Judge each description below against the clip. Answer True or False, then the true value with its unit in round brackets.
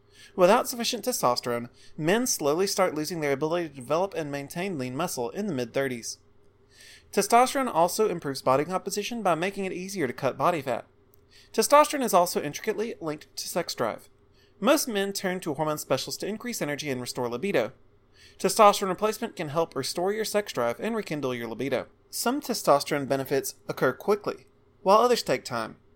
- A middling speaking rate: True (170 wpm)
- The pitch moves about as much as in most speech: False (7.5 semitones)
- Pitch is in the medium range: True (170 Hz)